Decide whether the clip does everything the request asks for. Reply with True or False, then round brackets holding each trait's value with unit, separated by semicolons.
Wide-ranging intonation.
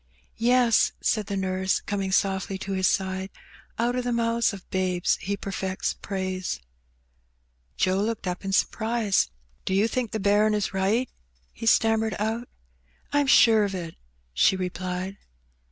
False (2.9 semitones)